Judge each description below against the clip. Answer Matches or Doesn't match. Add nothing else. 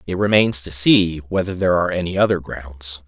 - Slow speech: Doesn't match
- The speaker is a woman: Doesn't match